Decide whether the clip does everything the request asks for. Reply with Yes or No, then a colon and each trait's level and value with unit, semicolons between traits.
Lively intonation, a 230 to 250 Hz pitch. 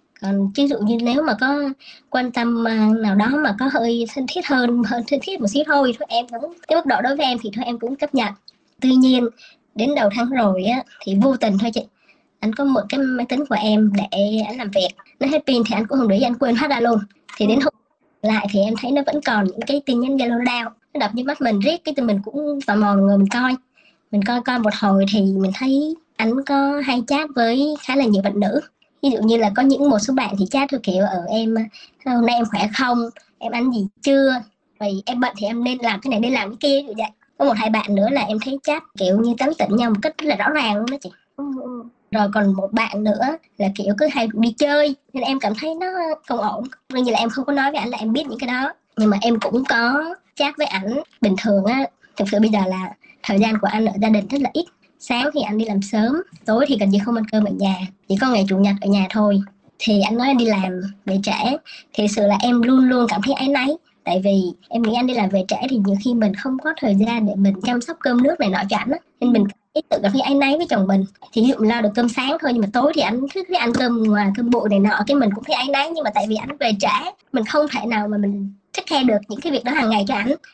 No: average, 4.8 semitones; high, 235 Hz